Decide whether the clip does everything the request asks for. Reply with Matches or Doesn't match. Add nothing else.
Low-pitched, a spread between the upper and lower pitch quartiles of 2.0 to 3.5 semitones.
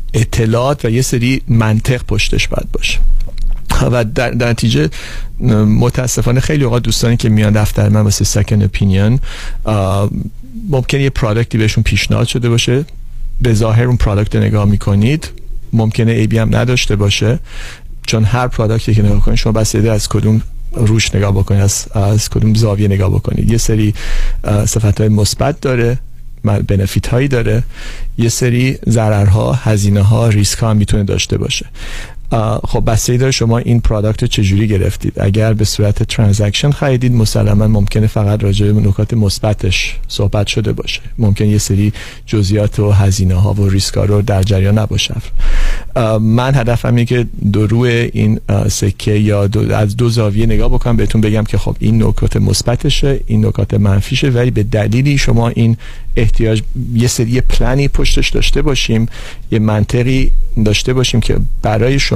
Matches